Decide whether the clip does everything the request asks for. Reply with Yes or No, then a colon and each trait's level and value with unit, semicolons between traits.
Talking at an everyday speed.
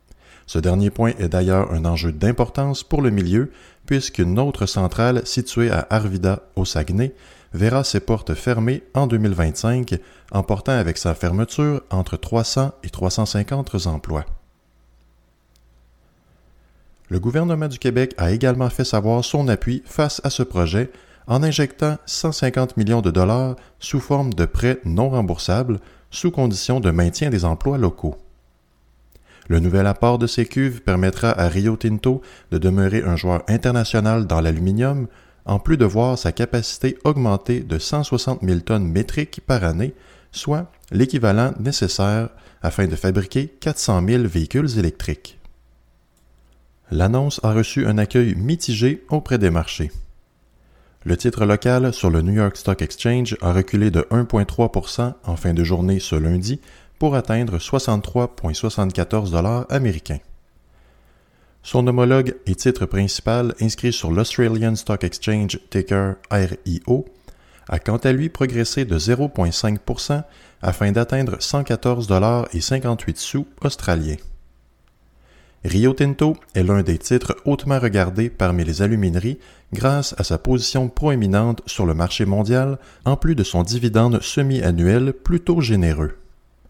No: slow, 135 wpm